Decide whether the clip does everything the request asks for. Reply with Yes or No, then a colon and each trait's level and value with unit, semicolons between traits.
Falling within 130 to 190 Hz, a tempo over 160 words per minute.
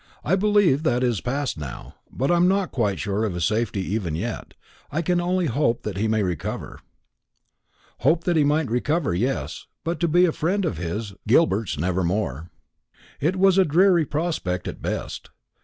Yes: low, 135 Hz; average, 185 wpm